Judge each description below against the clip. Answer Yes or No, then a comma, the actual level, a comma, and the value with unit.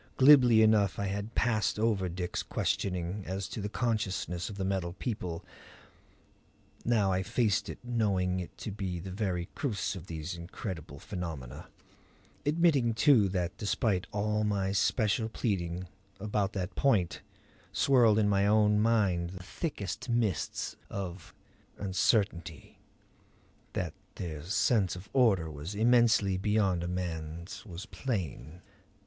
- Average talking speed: No, slow, 130 wpm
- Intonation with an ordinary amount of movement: Yes, average, 3.5 semitones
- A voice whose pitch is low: Yes, low, 100 Hz